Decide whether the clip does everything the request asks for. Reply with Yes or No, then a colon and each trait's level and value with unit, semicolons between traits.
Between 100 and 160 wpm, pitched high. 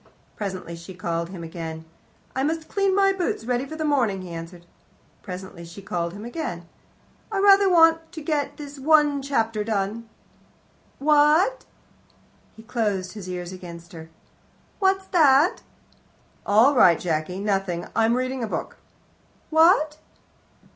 Yes: slow, 135 wpm; high, 225 Hz